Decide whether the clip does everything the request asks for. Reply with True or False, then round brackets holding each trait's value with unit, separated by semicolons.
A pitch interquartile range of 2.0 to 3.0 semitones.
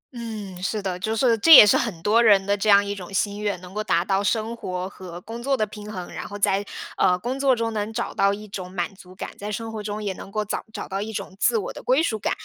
True (2.4 semitones)